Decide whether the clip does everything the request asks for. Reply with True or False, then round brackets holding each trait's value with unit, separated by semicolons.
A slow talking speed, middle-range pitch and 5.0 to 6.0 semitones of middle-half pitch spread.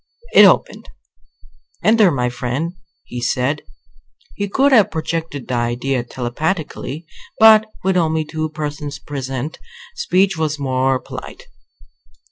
True (115 wpm; 150 Hz; 5.5 semitones)